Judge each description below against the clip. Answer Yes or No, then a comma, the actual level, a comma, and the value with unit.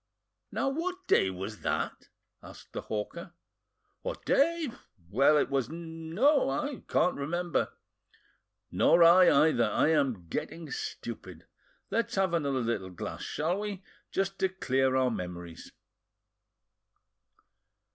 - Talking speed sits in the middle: No, slow, 115 wpm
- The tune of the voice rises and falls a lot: Yes, wide, 7.0 semitones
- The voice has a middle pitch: Yes, medium, 160 Hz